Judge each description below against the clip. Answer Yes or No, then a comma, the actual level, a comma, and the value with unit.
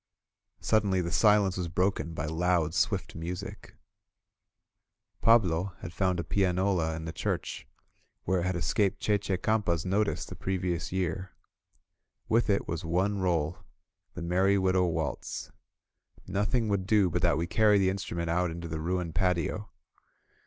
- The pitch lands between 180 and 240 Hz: No, very low, 90 Hz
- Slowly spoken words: No, average, 150 wpm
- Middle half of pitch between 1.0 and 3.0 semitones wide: Yes, narrow, 2.6 semitones